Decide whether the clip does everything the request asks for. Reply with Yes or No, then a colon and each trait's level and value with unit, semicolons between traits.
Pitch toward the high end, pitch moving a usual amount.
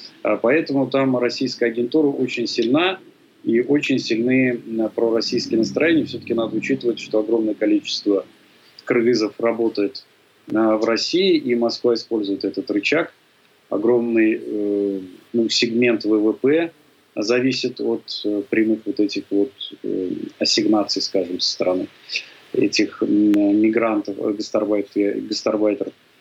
No: low, 115 Hz; average, 3.5 semitones